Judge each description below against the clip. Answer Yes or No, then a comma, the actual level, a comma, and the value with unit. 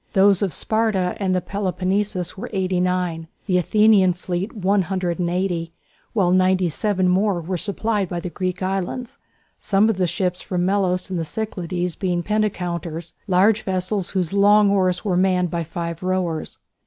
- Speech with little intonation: Yes, narrow, 2.1 semitones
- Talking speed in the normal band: Yes, average, 155 wpm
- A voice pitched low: No, medium, 185 Hz